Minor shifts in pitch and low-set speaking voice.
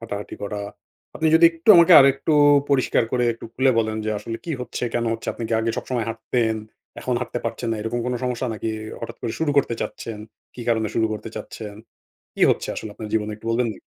Yes: narrow, 2.3 semitones; low, 115 Hz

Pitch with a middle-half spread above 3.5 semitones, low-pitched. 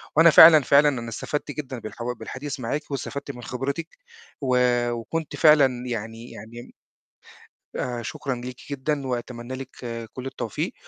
No: average, 3.2 semitones; low, 130 Hz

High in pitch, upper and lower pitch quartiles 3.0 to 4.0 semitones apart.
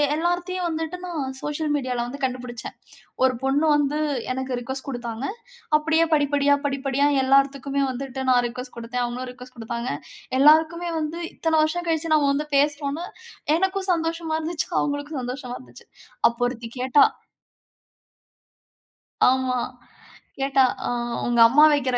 Yes: very high, 275 Hz; average, 3.7 semitones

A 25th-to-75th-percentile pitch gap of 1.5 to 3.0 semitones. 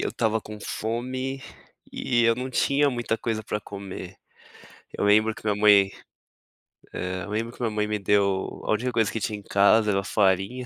Yes: average, 2.7 semitones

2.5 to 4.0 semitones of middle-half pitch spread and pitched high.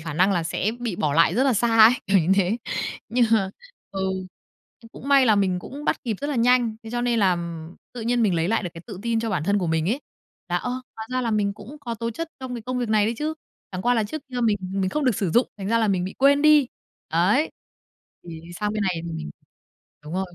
No: average, 4.8 semitones; high, 215 Hz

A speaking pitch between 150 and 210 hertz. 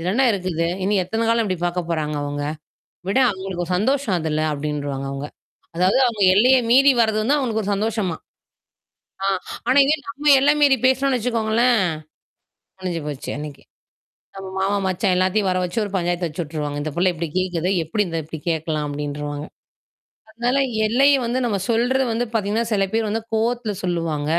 Yes: high, 195 Hz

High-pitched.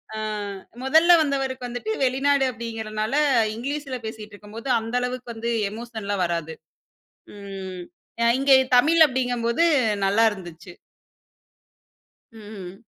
Yes: high, 230 Hz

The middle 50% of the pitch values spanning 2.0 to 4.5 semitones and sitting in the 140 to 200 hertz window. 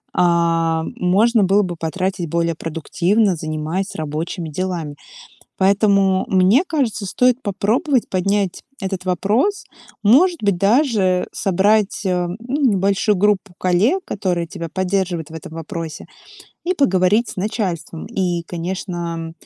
Yes: average, 3.5 semitones; high, 190 Hz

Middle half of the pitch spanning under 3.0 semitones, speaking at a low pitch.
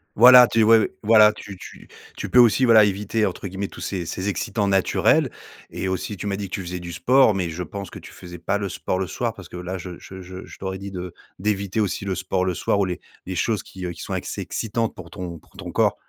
Yes: narrow, 2.6 semitones; very low, 95 Hz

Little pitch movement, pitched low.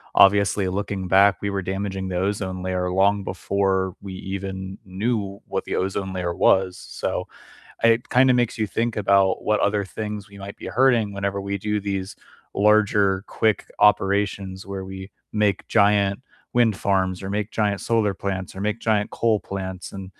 Yes: narrow, 1.6 semitones; low, 100 Hz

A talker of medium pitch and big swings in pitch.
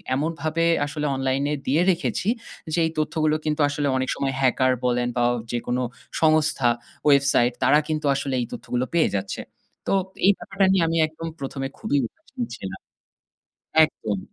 No: medium, 145 Hz; average, 3.6 semitones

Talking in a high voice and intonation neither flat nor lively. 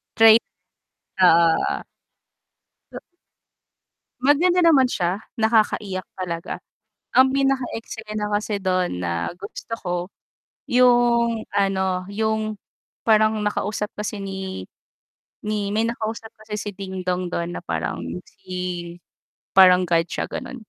Yes: high, 205 Hz; average, 3.4 semitones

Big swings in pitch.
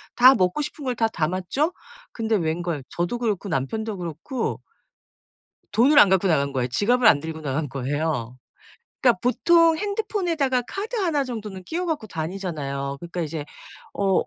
Yes: wide, 8.5 semitones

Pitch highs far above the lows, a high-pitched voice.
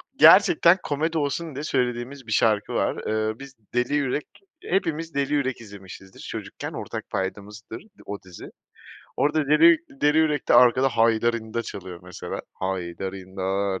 No: wide, 6.4 semitones; low, 120 Hz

